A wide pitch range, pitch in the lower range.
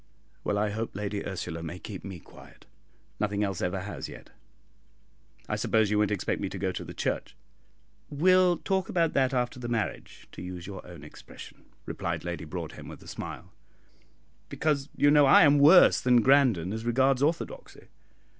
Yes: wide, 6.8 semitones; low, 110 Hz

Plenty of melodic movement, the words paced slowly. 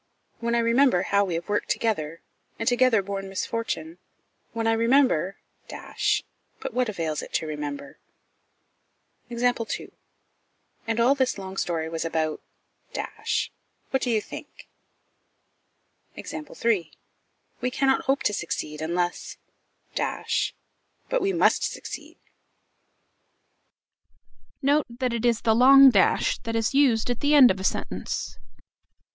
Yes: wide, 6.1 semitones; slow, 120 wpm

